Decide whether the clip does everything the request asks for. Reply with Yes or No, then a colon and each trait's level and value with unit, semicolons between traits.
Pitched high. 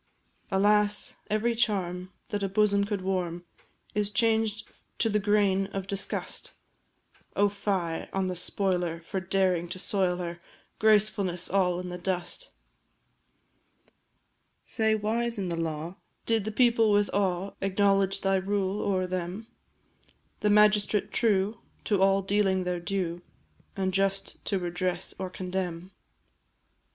Yes: high, 195 Hz